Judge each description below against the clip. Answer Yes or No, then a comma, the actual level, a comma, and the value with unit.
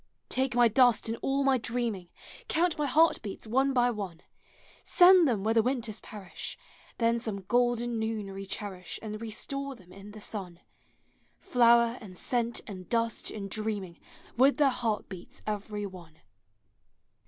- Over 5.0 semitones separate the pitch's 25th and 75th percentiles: No, average, 3.5 semitones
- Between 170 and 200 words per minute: No, average, 155 wpm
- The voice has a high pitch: Yes, high, 225 Hz